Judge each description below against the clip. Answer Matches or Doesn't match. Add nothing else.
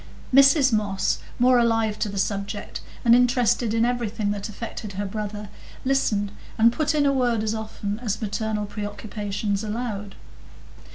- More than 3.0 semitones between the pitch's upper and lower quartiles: Doesn't match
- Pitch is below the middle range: Doesn't match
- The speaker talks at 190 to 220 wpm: Doesn't match